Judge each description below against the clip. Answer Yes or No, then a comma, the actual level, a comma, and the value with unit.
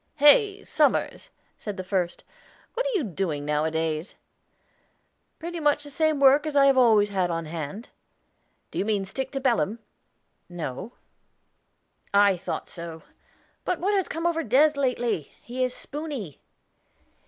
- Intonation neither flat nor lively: No, wide, 8.7 semitones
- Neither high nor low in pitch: No, high, 235 Hz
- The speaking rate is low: No, average, 145 wpm